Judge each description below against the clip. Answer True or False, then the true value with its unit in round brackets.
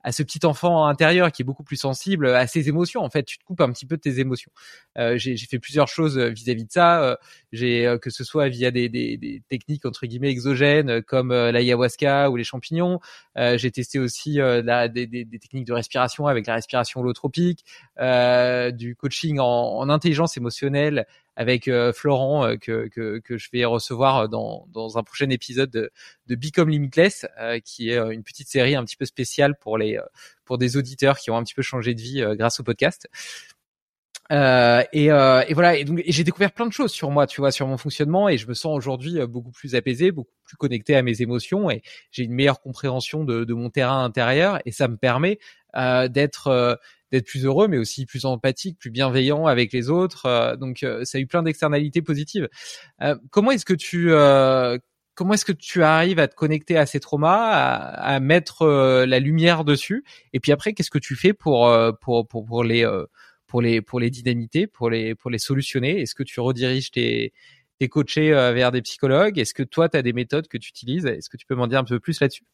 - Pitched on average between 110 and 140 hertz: True (135 Hz)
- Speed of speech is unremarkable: False (225 wpm)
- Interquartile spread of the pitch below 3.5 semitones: False (3.8 semitones)